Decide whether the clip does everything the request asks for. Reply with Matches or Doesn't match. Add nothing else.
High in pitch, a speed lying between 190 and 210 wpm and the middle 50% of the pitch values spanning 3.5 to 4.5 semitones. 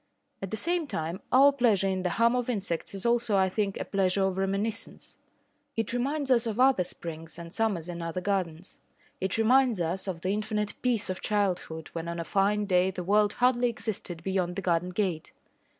Matches